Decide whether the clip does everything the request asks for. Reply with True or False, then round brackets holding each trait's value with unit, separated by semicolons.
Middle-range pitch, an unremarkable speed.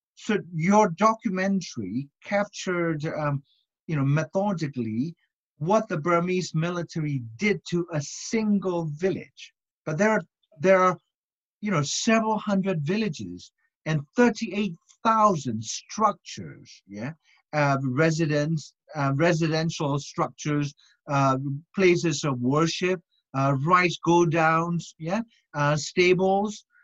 False (170 Hz; 105 wpm)